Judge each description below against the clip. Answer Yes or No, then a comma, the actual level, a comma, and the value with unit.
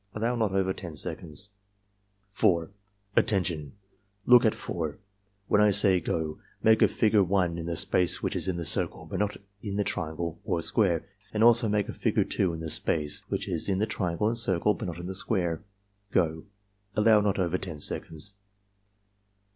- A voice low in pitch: Yes, very low, 95 Hz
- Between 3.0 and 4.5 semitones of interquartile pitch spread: Yes, average, 3.8 semitones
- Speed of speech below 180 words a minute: No, average, 185 wpm